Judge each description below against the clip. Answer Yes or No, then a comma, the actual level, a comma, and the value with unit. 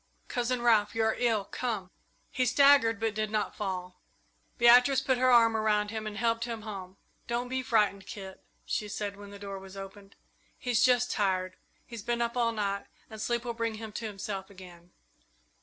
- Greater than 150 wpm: Yes, average, 190 wpm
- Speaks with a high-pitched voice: Yes, high, 220 Hz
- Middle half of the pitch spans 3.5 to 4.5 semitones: No, average, 3.0 semitones